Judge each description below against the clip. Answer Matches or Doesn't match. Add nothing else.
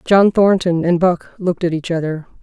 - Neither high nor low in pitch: Matches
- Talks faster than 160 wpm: Matches